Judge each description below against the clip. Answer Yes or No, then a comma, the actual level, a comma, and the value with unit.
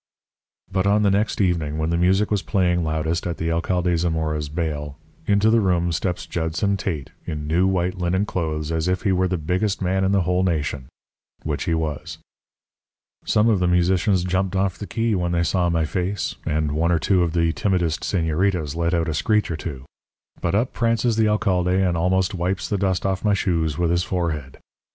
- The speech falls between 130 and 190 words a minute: No, average, 200 wpm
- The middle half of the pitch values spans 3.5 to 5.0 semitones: No, average, 2.8 semitones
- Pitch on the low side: Yes, very low, 90 Hz